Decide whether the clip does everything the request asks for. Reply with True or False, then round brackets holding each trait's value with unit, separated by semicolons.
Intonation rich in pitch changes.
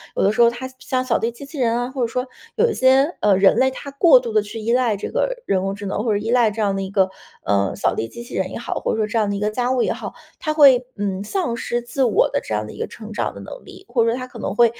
False (3.8 semitones)